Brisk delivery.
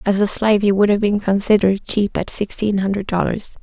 Yes: fast, 215 wpm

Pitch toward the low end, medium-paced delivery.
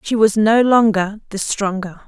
No: high, 210 Hz; average, 175 wpm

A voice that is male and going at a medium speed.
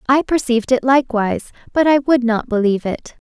No: female; average, 185 wpm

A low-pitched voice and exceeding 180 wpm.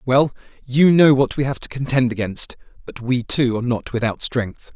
Yes: low, 125 Hz; average, 200 wpm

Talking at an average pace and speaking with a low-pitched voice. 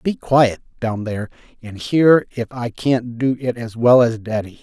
Yes: average, 195 wpm; low, 120 Hz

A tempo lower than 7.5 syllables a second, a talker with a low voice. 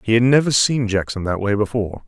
Yes: 6.2 syllables/s; low, 110 Hz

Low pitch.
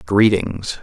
Yes: very low, 95 Hz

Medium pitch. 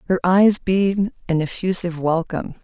Yes: medium, 180 Hz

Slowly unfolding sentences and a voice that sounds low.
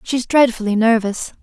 No: slow, 125 wpm; high, 230 Hz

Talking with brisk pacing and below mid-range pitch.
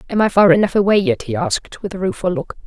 No: fast, 270 wpm; high, 190 Hz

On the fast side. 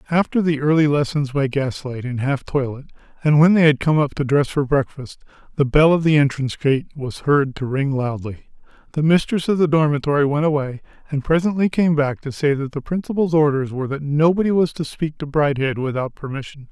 Yes: fast, 210 wpm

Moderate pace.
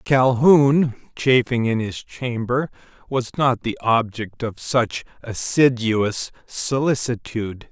No: slow, 100 wpm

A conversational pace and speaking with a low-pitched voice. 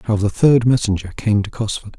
No: fast, 210 wpm; low, 110 Hz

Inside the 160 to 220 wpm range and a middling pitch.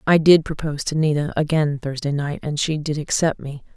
Yes: fast, 205 wpm; medium, 150 Hz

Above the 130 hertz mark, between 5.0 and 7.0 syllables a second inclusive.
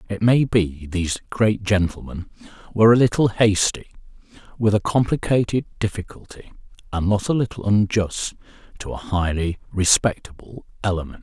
No: low, 100 Hz; 5.2 syllables/s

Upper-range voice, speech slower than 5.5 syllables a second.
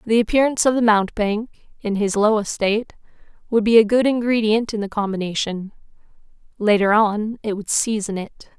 No: high, 215 Hz; 5.6 syllables/s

